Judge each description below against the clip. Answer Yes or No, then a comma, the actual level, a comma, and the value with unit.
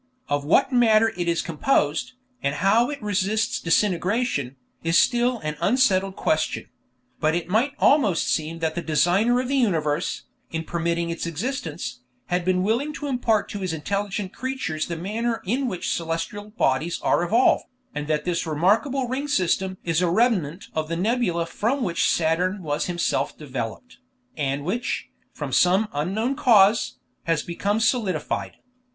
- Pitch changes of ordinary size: No, wide, 5.9 semitones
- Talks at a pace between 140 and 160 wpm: Yes, average, 155 wpm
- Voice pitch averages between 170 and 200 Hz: Yes, medium, 185 Hz